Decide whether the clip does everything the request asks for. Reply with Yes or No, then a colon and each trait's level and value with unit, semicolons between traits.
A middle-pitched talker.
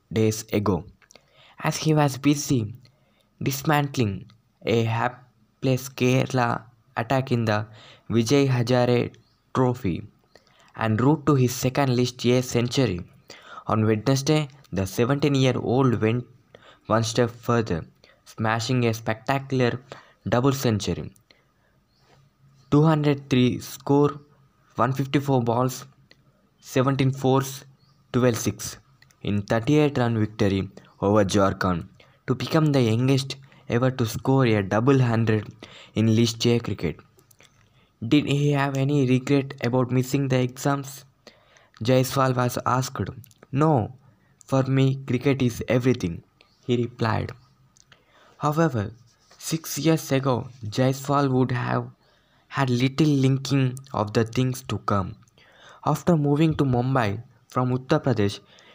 No: low, 125 Hz